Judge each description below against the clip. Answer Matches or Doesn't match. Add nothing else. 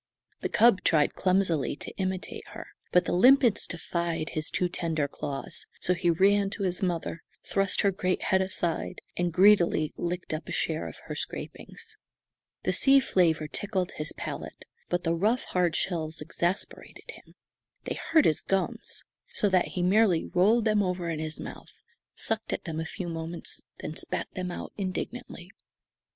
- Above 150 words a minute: Matches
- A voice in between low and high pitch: Matches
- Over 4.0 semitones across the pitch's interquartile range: Doesn't match